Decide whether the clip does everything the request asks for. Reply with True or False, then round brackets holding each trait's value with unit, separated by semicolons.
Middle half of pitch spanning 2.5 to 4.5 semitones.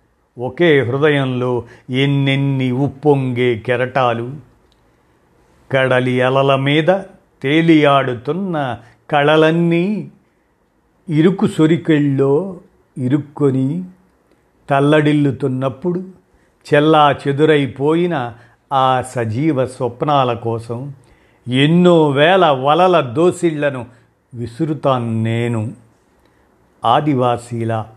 True (4.0 semitones)